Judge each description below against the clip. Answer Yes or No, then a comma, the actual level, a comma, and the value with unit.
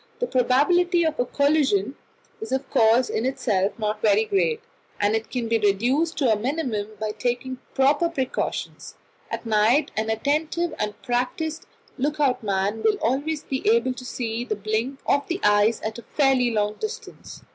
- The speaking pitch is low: No, very high, 250 Hz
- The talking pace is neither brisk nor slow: Yes, average, 170 wpm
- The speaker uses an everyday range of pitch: Yes, average, 4.8 semitones